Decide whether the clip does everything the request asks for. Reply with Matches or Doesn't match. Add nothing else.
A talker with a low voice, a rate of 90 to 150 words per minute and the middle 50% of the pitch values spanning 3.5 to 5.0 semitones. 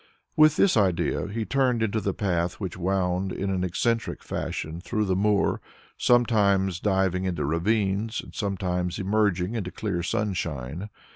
Doesn't match